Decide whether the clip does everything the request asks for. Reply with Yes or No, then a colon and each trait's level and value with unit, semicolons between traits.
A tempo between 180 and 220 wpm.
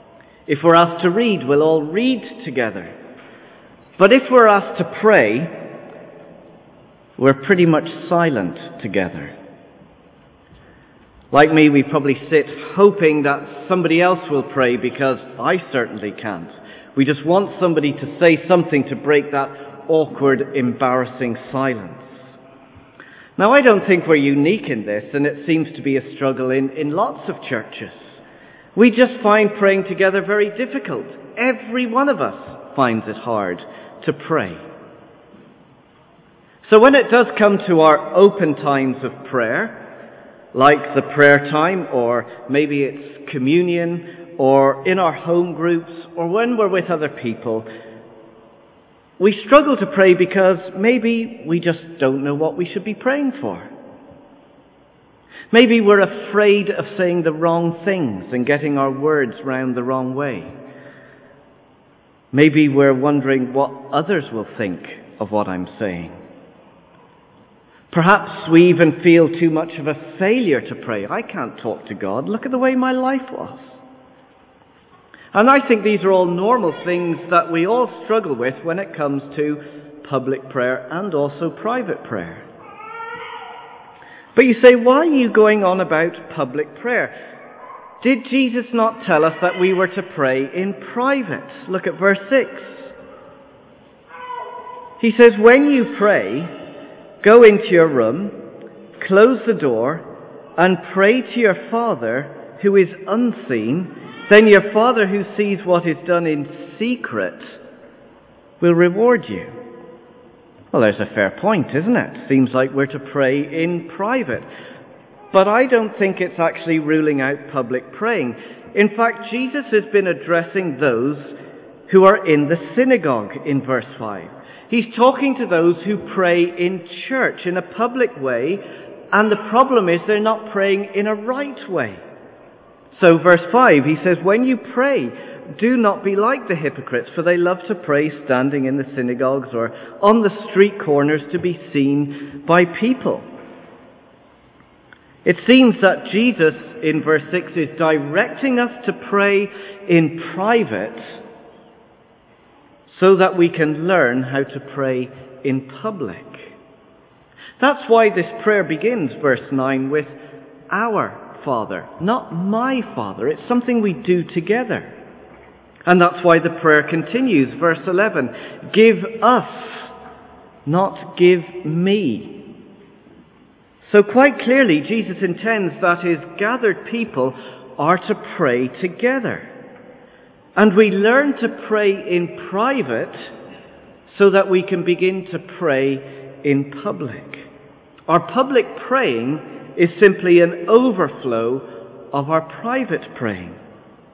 No: average, 140 wpm